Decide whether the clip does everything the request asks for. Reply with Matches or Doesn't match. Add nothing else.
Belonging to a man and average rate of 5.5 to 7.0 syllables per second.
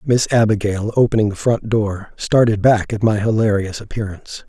Doesn't match